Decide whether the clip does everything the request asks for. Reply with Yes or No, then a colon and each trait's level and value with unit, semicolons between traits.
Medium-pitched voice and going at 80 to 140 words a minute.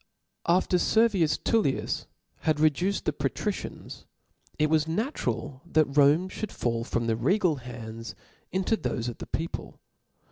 Yes: medium, 155 Hz; slow, 135 wpm